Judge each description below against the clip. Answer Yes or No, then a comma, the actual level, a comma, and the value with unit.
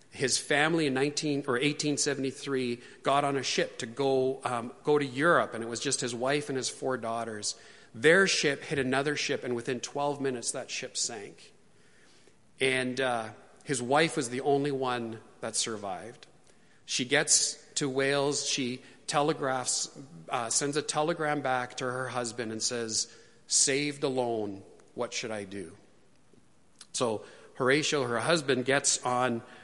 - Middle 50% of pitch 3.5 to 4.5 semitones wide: No, average, 2.9 semitones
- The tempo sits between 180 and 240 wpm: No, average, 160 wpm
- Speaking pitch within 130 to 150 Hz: Yes, low, 135 Hz